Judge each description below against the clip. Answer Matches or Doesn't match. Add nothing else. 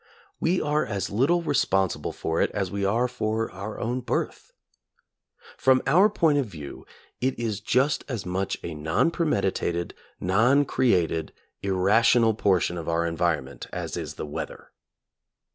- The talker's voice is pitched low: Matches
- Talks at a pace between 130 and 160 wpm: Matches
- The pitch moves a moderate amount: Doesn't match